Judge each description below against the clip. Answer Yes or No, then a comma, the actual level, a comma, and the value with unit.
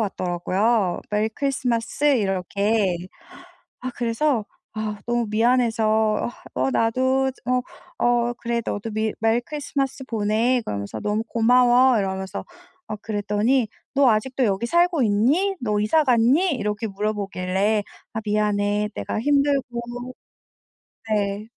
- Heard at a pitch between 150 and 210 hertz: No, high, 225 Hz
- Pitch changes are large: No, average, 3.4 semitones